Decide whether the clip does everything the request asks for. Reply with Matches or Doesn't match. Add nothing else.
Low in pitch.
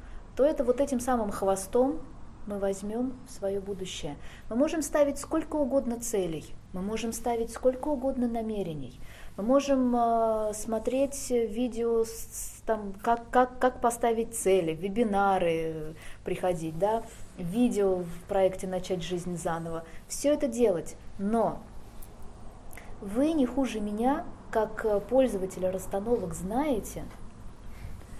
Doesn't match